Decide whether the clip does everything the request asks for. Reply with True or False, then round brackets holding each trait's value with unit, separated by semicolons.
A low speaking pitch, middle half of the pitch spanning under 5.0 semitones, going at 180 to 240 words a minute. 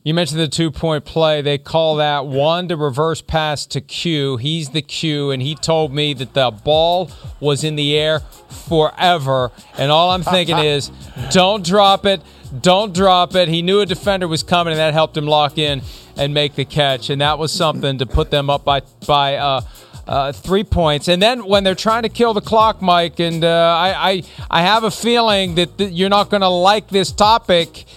False (160 Hz; 4.1 semitones; 205 wpm)